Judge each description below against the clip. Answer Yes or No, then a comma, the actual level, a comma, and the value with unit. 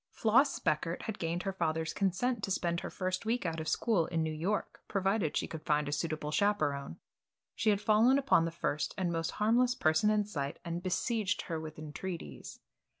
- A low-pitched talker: No, medium, 175 Hz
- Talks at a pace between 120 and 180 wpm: No, average, 195 wpm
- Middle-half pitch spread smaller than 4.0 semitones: No, average, 4.9 semitones